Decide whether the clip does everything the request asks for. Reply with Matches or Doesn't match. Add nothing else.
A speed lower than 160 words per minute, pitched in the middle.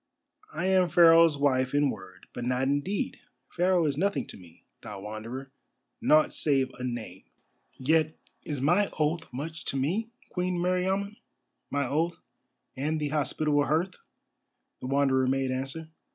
Matches